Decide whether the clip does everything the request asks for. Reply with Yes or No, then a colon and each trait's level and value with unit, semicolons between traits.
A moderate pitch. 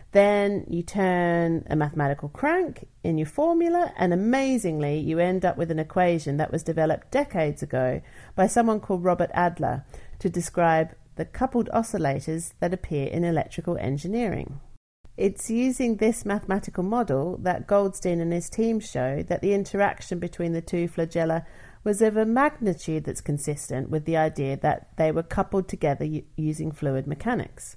Yes: medium, 175 Hz